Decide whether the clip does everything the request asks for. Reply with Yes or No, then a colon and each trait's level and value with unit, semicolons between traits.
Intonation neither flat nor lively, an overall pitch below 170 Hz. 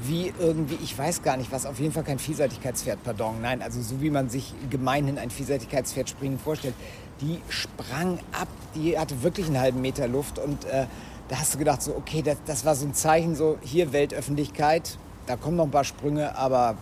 Yes: average, 3.2 semitones; medium, 140 Hz